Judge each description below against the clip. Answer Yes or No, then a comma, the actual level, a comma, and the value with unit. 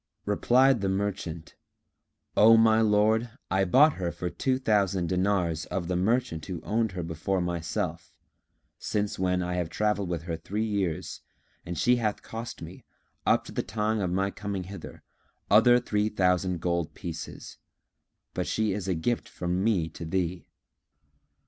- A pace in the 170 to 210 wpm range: No, average, 160 wpm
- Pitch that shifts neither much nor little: Yes, average, 3.5 semitones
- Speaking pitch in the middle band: No, very low, 95 Hz